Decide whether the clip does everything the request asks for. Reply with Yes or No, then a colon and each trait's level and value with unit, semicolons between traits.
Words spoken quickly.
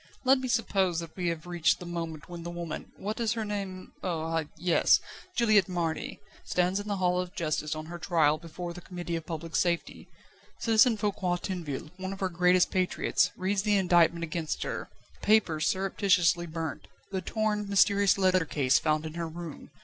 No: average, 190 wpm